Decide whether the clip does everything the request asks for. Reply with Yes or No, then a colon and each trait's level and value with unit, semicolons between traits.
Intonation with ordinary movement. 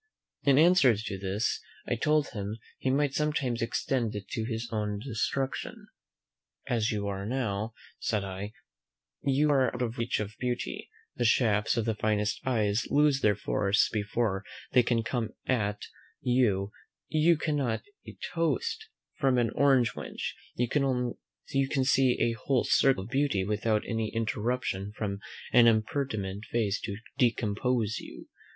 Yes: average, 4.1 semitones